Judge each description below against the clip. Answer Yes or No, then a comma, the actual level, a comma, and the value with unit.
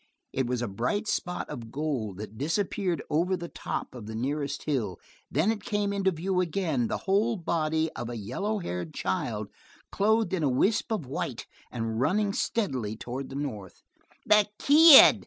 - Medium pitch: Yes, medium, 155 Hz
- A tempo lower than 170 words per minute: No, average, 175 wpm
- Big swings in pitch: Yes, wide, 8.7 semitones